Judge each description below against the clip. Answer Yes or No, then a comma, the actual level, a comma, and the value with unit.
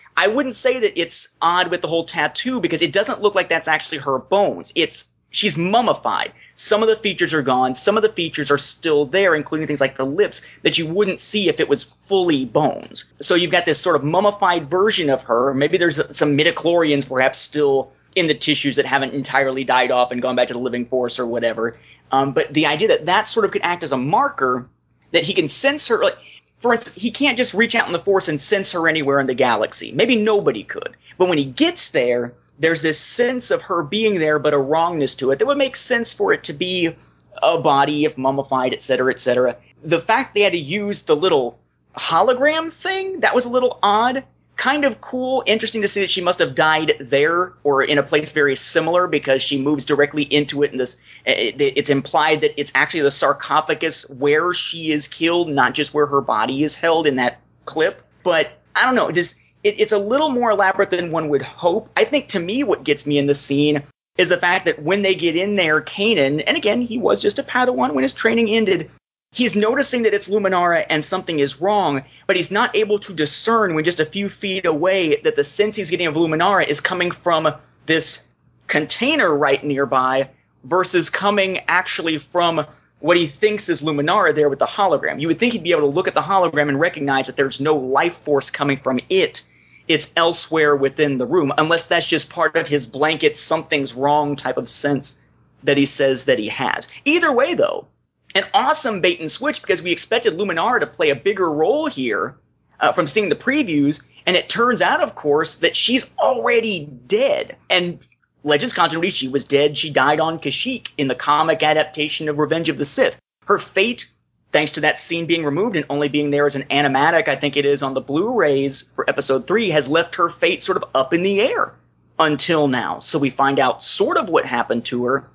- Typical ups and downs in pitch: No, wide, 6.3 semitones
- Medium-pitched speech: Yes, medium, 165 Hz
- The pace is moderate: No, fast, 220 wpm